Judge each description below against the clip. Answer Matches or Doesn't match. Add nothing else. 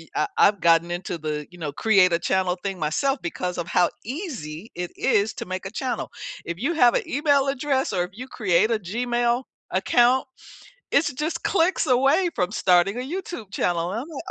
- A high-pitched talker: Matches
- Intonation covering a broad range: Matches